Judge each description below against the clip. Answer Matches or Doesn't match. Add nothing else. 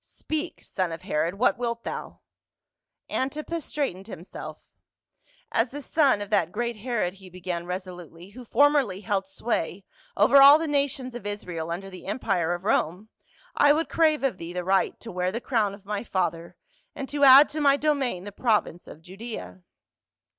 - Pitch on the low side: Doesn't match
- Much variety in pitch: Matches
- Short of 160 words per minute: Doesn't match